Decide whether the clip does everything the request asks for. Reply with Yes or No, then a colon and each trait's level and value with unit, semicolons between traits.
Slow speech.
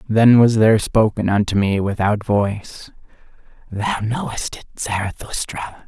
Yes: slow, 120 wpm